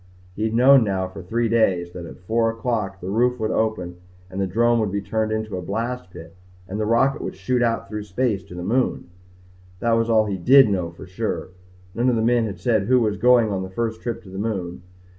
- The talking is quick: Yes, fast, 235 wpm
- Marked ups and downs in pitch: No, average, 3.7 semitones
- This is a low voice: Yes, low, 110 Hz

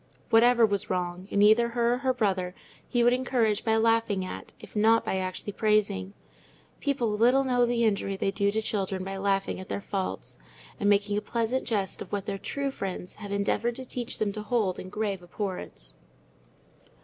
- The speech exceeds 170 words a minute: Yes, average, 190 wpm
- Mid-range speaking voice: No, high, 210 Hz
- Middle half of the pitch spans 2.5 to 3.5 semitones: Yes, average, 3.2 semitones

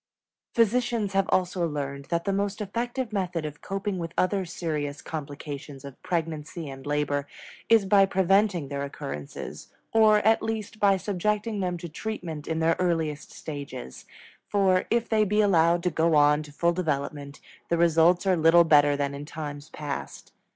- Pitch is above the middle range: No, medium, 170 Hz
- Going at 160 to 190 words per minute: Yes, average, 165 wpm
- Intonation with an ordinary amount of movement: Yes, average, 5.0 semitones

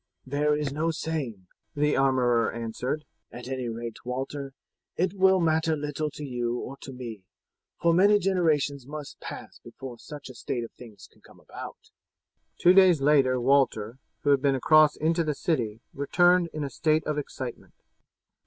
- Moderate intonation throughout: Yes, average, 3.9 semitones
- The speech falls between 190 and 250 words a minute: No, average, 165 wpm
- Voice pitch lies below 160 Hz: Yes, medium, 140 Hz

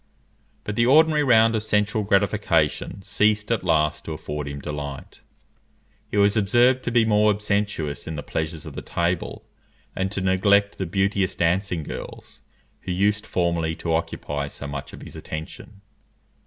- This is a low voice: Yes, very low, 95 Hz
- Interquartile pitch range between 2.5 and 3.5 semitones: No, average, 4.7 semitones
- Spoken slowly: No, average, 160 wpm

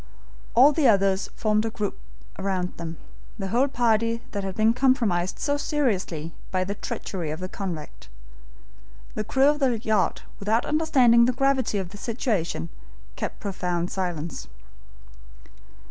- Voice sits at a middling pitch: No, high, 210 Hz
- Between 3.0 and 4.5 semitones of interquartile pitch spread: No, average, 4.9 semitones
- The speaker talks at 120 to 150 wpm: Yes, average, 145 wpm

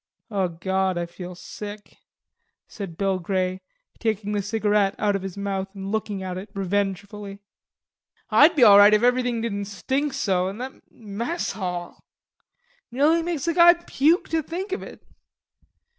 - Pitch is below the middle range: No, high, 205 Hz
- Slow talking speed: No, average, 160 wpm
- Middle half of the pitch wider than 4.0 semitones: Yes, average, 4.4 semitones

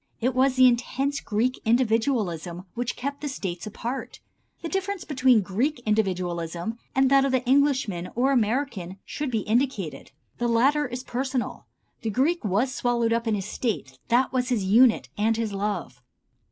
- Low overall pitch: No, high, 240 Hz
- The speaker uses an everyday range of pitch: Yes, average, 4.1 semitones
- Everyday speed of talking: Yes, average, 165 wpm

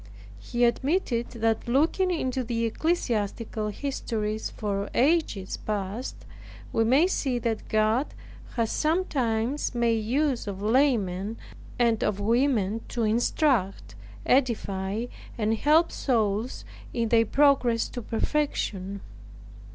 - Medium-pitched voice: No, high, 230 Hz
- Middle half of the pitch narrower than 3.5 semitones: No, average, 3.9 semitones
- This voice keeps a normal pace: No, slow, 110 wpm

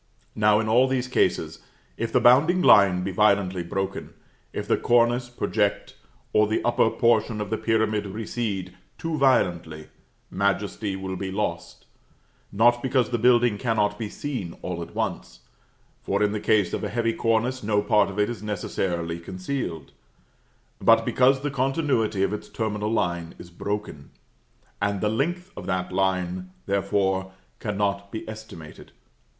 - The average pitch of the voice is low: Yes, low, 105 Hz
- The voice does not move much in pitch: No, average, 3.8 semitones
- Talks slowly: No, average, 155 wpm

